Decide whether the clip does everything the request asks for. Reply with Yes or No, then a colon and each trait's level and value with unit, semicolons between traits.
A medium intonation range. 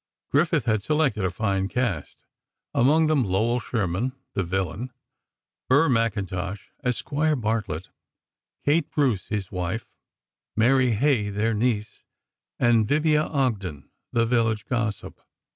Yes: average, 4.9 semitones